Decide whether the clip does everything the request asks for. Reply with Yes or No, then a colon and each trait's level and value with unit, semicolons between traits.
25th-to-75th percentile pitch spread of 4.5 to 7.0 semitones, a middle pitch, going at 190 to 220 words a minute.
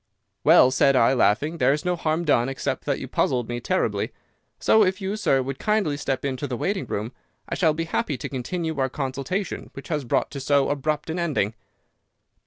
No: average, 4.1 semitones; medium, 145 Hz; average, 200 wpm